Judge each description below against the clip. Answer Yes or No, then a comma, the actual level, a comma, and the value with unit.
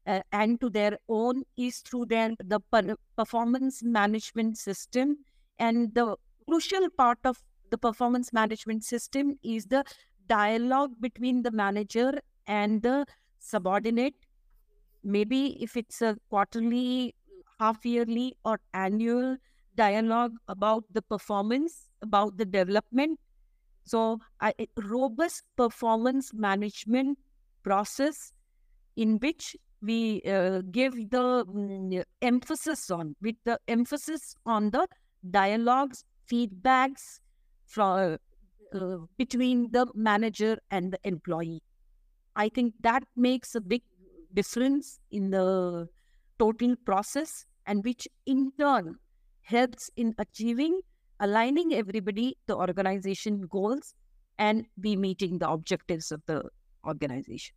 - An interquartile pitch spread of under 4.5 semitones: Yes, average, 3.8 semitones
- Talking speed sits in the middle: No, slow, 110 wpm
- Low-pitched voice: No, high, 225 Hz